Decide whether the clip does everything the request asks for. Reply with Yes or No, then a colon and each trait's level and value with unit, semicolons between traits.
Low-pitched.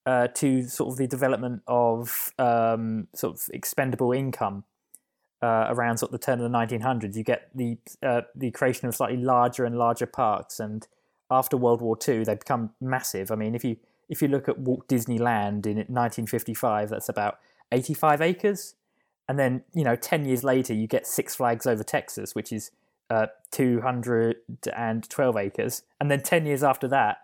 Yes: low, 120 Hz